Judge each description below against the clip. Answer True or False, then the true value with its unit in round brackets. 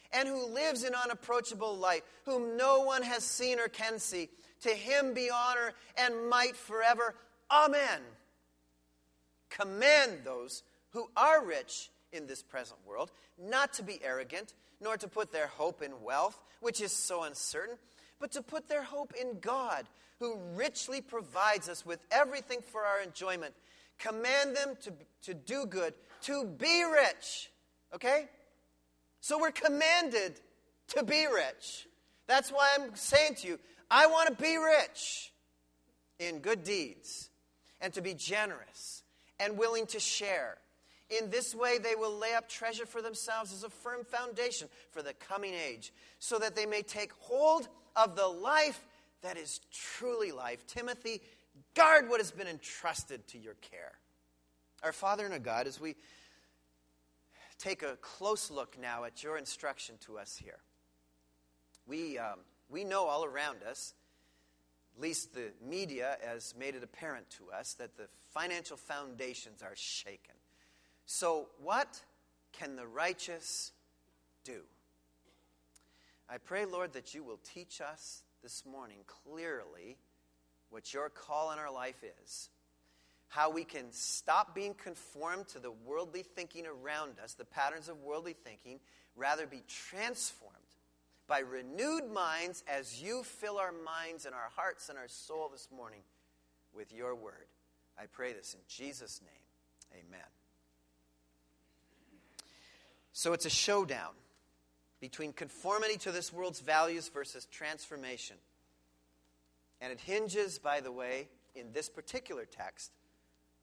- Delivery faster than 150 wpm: False (145 wpm)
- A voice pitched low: False (170 Hz)